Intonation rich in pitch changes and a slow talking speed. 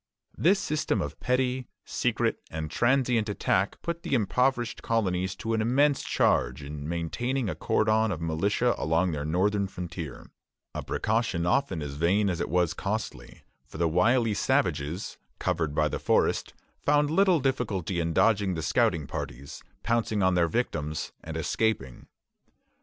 No: wide, 6.6 semitones; average, 150 wpm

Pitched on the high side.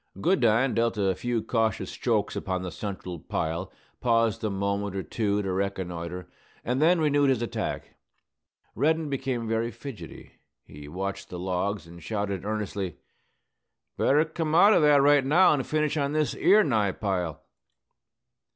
No: low, 110 Hz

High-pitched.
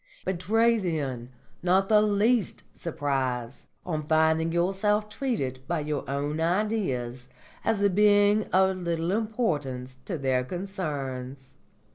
No: medium, 170 Hz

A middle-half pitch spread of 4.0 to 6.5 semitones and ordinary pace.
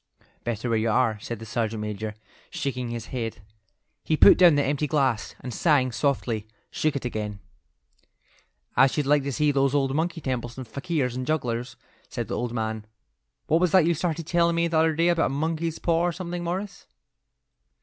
Yes: wide, 5.5 semitones; average, 190 wpm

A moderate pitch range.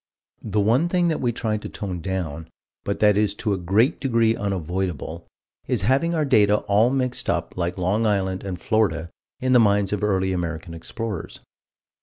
Yes: average, 3.9 semitones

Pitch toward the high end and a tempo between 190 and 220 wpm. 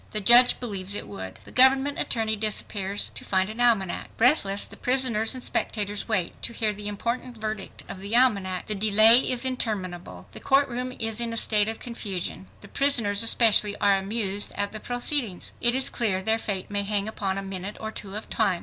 Yes: high, 215 Hz; average, 200 wpm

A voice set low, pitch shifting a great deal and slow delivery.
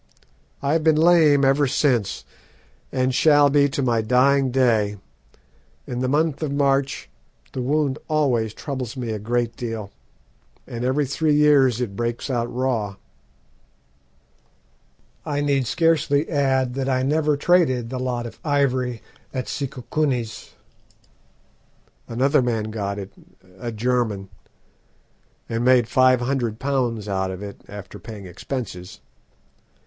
No: low, 130 Hz; average, 3.5 semitones; slow, 130 wpm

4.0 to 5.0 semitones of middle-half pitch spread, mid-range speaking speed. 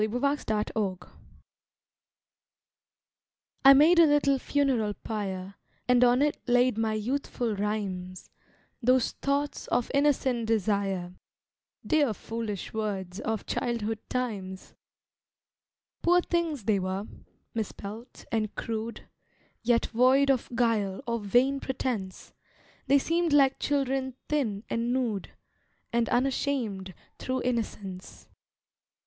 No: average, 4.5 semitones; slow, 105 wpm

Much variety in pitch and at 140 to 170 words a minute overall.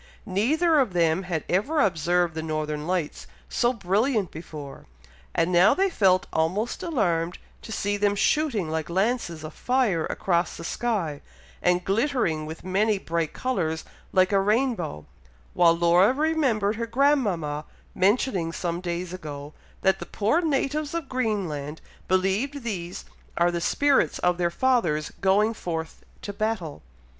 Yes: wide, 5.8 semitones; average, 145 wpm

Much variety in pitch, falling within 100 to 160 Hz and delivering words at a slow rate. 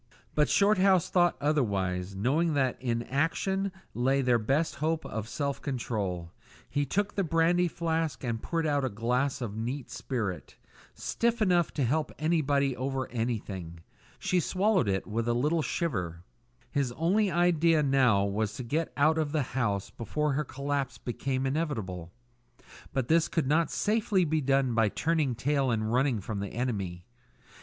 No: wide, 5.7 semitones; low, 135 Hz; average, 160 wpm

